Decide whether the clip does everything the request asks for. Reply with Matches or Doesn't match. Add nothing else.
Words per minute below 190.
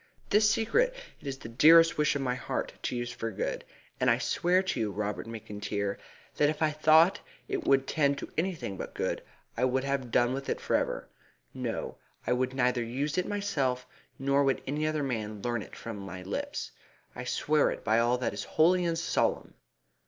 Doesn't match